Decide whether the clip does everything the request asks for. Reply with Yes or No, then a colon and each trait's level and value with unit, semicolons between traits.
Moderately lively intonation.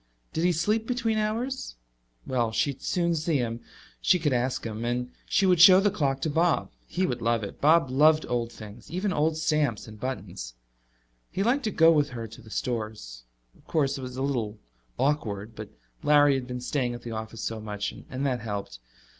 No: wide, 6.2 semitones